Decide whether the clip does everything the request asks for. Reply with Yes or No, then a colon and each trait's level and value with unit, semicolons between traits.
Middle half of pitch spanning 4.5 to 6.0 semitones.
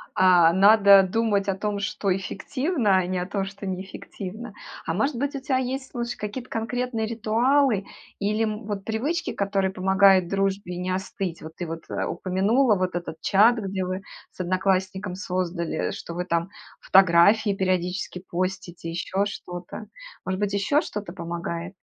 No: average, 3.0 semitones